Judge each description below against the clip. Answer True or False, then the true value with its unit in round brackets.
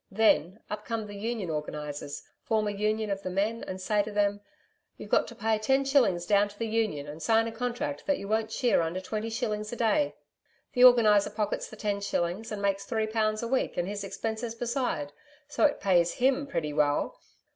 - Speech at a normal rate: False (210 wpm)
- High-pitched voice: True (215 Hz)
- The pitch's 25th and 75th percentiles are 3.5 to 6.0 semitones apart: False (2.6 semitones)